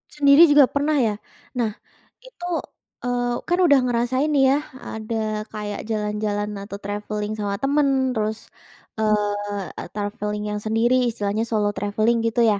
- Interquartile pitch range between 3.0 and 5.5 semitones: Yes, average, 3.6 semitones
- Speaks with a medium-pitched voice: No, high, 220 Hz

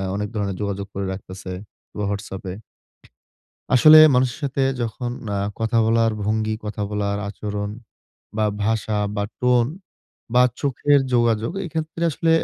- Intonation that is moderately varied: Yes, average, 3.4 semitones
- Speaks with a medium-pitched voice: No, low, 110 Hz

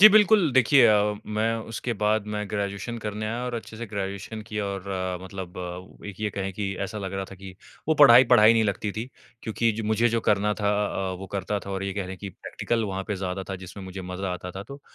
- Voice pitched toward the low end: Yes, low, 105 Hz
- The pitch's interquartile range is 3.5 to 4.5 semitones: No, average, 2.7 semitones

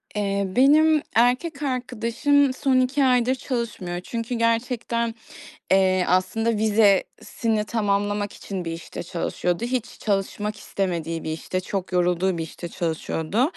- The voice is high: Yes, high, 215 Hz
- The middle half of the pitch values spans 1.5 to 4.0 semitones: No, average, 5.0 semitones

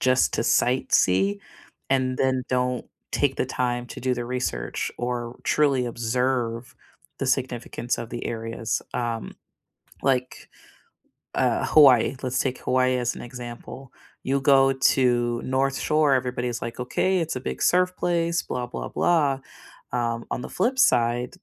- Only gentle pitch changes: Yes, narrow, 2.0 semitones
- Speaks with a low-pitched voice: Yes, low, 125 Hz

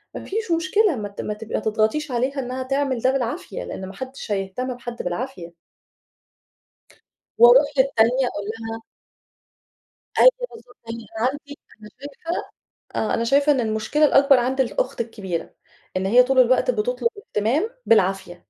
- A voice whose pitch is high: Yes, very high, 250 Hz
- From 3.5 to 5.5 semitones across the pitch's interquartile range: Yes, average, 4.2 semitones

